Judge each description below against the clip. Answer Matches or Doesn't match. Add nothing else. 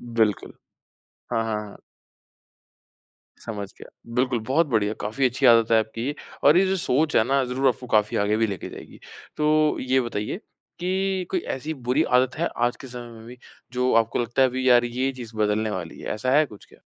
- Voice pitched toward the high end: Doesn't match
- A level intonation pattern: Doesn't match